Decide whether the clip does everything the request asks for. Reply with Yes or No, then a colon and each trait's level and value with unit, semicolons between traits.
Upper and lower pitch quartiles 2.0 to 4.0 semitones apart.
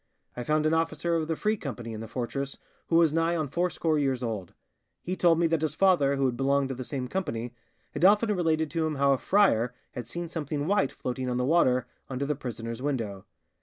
No: average, 4.7 semitones